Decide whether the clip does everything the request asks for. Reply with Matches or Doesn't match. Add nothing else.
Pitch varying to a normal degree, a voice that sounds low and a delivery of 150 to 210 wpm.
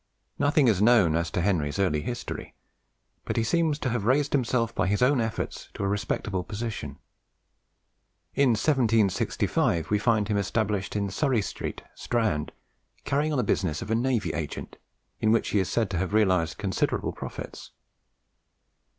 Matches